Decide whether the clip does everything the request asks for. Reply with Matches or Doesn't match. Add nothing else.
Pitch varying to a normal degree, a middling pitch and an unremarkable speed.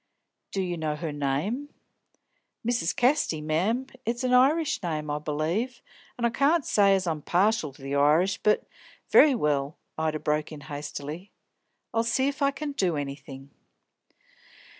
Doesn't match